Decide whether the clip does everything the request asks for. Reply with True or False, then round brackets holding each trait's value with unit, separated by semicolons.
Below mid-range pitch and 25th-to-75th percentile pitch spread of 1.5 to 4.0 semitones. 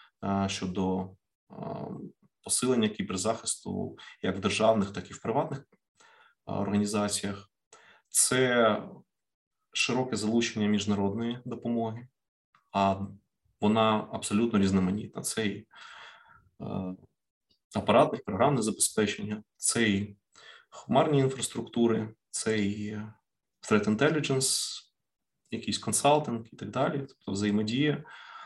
True (110 Hz; 2.8 semitones)